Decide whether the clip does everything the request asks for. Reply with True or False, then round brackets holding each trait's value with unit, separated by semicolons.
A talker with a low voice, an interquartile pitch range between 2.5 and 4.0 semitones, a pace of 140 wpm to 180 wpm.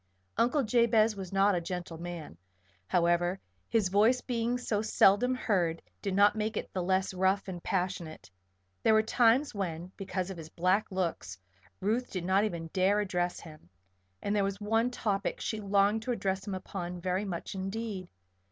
False (195 Hz; 3.3 semitones; 170 wpm)